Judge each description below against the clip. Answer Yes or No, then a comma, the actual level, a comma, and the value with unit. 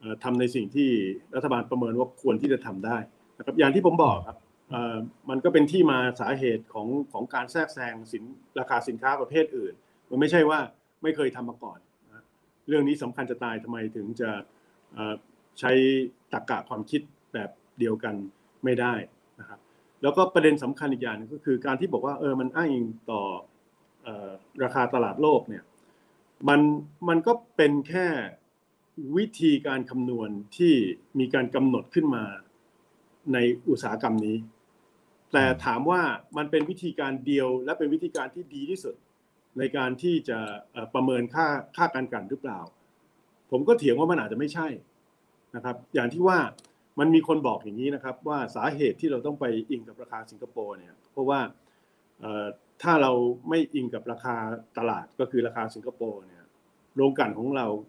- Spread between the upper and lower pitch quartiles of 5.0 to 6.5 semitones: No, average, 4.2 semitones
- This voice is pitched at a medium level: No, low, 130 Hz